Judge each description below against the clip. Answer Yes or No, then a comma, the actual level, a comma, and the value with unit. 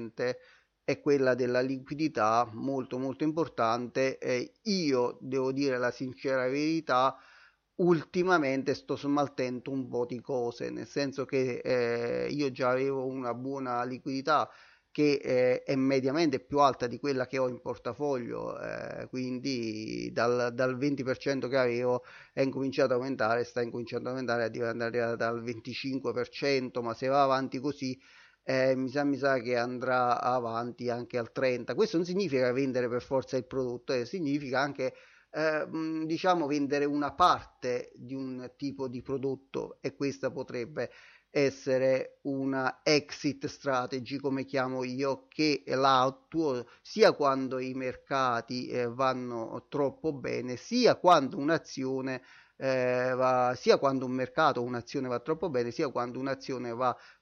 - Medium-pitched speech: No, low, 130 Hz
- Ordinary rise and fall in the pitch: No, narrow, 2.1 semitones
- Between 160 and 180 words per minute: No, average, 145 wpm